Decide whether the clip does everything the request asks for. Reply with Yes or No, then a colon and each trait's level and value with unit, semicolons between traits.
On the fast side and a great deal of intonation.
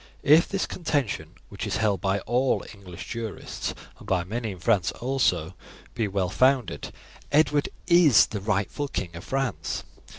No: average, 155 wpm; wide, 6.2 semitones